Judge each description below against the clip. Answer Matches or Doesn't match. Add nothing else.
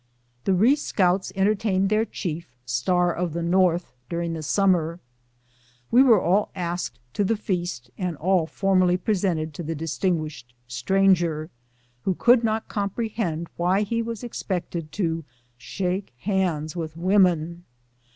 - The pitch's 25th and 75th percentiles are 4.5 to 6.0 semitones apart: Doesn't match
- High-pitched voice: Doesn't match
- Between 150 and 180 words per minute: Doesn't match